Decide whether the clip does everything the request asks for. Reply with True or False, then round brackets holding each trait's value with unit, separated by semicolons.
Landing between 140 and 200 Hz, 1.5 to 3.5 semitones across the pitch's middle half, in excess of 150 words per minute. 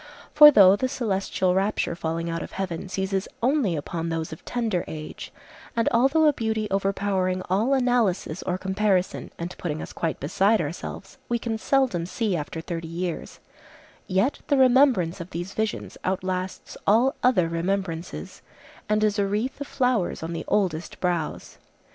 False (190 Hz; 4.8 semitones; 160 wpm)